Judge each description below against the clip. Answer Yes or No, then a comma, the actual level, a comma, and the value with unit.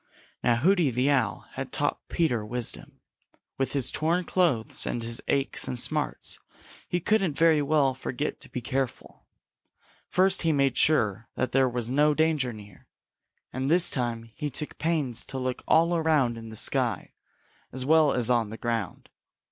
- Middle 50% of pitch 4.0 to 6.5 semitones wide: Yes, average, 4.8 semitones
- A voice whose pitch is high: No, low, 135 Hz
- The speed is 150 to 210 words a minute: Yes, average, 165 wpm